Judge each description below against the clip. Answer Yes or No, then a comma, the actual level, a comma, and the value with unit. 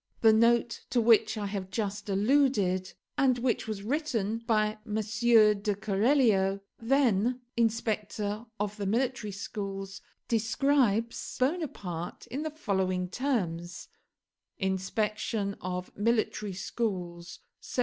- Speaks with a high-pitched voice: Yes, high, 215 Hz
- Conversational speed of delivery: No, slow, 110 wpm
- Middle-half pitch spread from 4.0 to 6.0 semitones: No, average, 3.3 semitones